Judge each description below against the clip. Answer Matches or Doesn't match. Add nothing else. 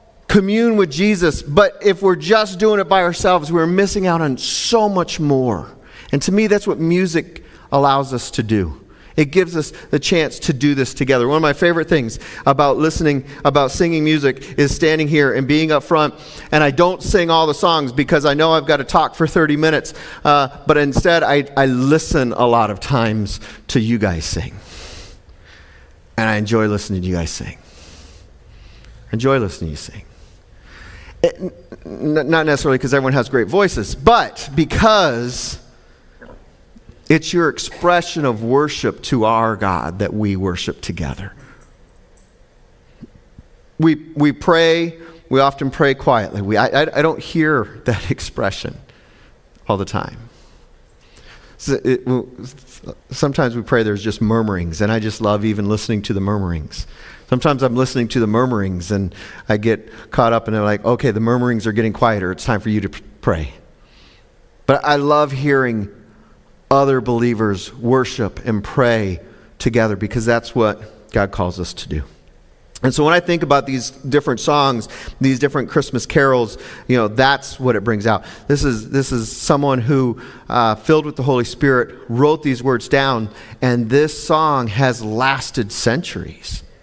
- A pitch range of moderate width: Doesn't match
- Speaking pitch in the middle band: Doesn't match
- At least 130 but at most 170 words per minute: Matches